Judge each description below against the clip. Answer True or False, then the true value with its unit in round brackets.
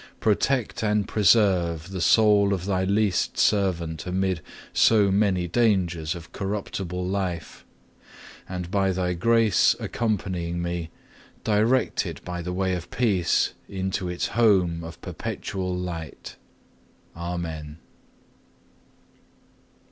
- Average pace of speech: False (110 wpm)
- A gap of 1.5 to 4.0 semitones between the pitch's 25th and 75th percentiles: True (2.8 semitones)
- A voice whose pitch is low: True (95 Hz)